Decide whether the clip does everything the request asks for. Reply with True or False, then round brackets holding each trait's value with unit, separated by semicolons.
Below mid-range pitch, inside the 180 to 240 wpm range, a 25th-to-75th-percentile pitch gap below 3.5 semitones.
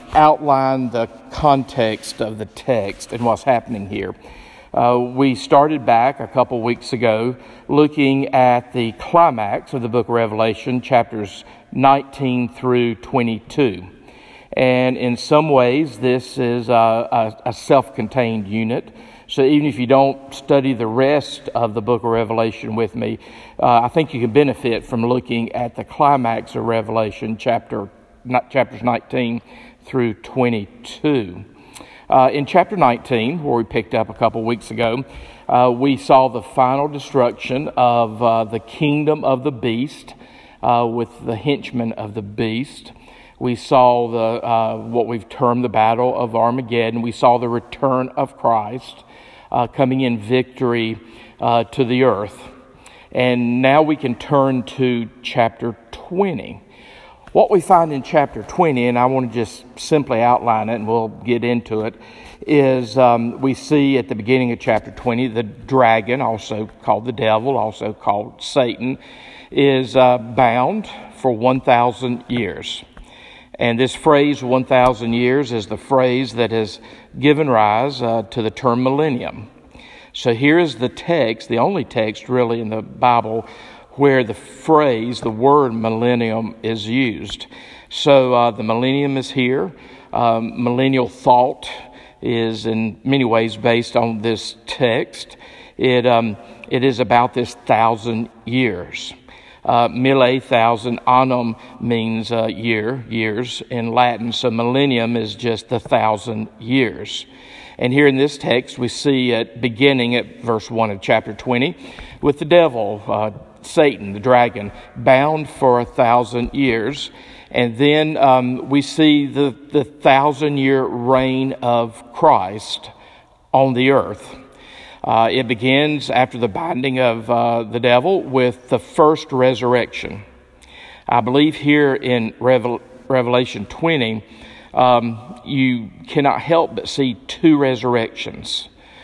False (125 Hz; 145 wpm; 2.5 semitones)